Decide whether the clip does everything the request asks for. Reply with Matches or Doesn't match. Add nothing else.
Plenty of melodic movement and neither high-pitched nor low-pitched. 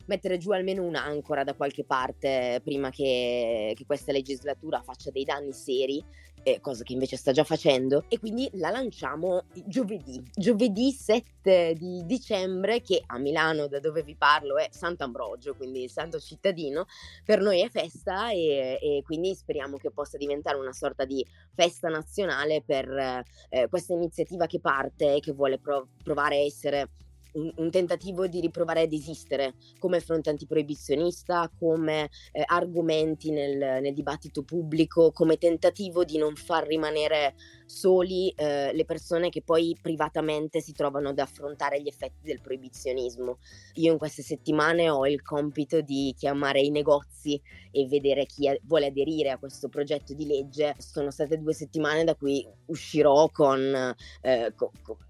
Doesn't match